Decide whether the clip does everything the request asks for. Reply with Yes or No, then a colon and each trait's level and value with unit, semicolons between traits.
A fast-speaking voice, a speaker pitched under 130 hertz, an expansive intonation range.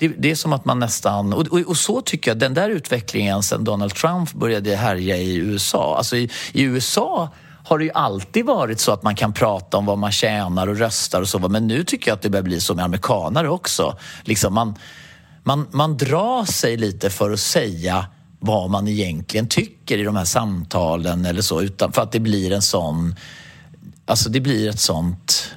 Yes: fast, 210 wpm; low, 110 Hz; wide, 5.7 semitones